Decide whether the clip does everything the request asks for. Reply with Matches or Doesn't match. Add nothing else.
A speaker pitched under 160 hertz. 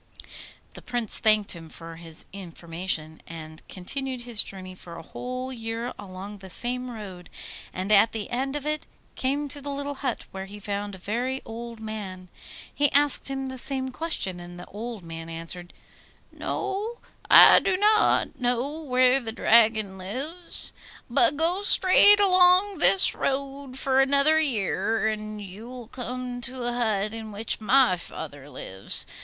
Doesn't match